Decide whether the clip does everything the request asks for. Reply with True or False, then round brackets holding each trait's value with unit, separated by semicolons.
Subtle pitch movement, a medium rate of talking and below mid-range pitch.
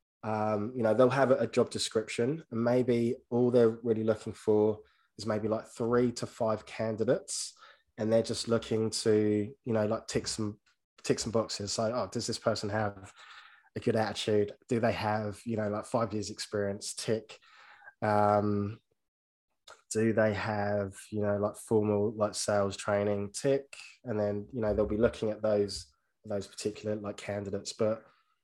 True (1.8 semitones; 170 wpm; 110 Hz)